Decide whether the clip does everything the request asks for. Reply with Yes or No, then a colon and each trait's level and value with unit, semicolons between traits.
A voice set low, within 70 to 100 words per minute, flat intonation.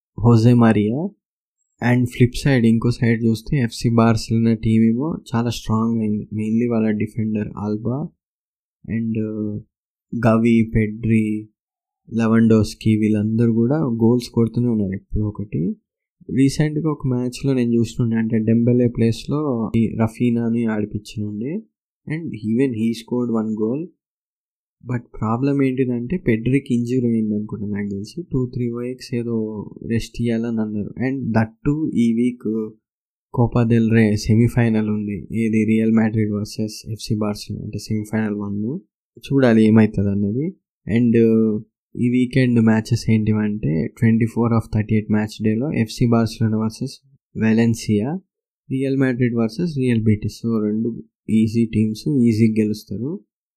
No: low, 115 Hz; fast, 125 wpm; narrow, 2.0 semitones